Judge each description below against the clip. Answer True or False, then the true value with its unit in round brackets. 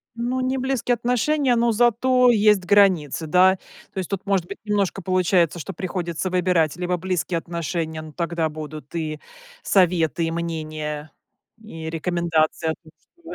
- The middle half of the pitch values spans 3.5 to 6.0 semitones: True (4.2 semitones)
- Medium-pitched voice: True (180 Hz)